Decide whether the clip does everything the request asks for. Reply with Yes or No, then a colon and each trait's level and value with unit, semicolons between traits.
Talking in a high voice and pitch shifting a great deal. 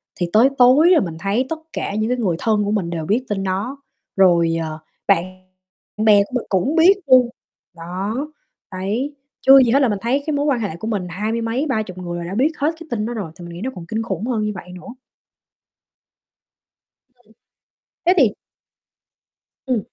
Yes: high, 220 Hz; wide, 5.7 semitones